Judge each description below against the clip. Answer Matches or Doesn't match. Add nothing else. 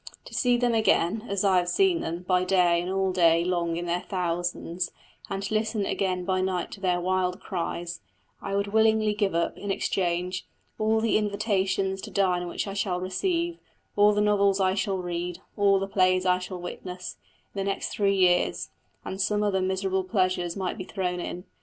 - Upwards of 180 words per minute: Matches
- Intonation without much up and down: Matches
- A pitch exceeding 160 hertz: Matches